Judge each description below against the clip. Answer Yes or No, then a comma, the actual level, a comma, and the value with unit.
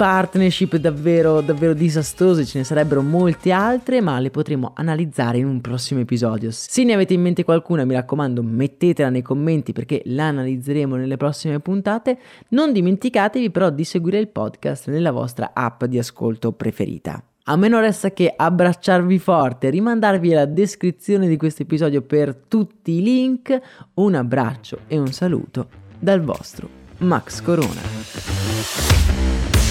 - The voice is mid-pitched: Yes, medium, 155 Hz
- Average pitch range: No, wide, 6.4 semitones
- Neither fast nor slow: Yes, average, 145 wpm